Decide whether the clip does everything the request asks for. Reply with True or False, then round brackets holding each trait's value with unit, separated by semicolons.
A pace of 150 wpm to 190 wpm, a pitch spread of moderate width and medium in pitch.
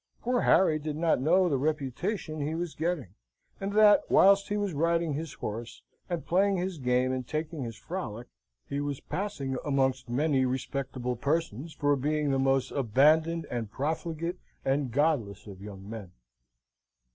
True (160 wpm; 4.5 semitones; 145 Hz)